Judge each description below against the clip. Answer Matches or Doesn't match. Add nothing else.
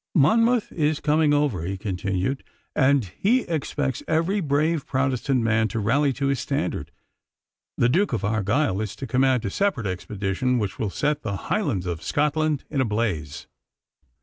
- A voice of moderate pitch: Doesn't match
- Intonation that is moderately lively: Doesn't match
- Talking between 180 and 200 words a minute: Doesn't match